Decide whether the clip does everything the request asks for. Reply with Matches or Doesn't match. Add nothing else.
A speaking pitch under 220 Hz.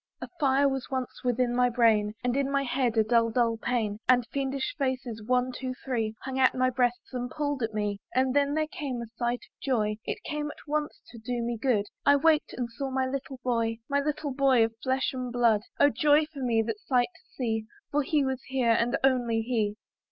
Doesn't match